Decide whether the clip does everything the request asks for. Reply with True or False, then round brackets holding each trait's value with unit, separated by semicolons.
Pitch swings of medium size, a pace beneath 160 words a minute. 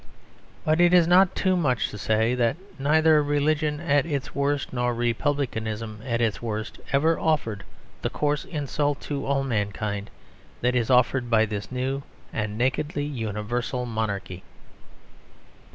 True (4.8 semitones; 140 wpm)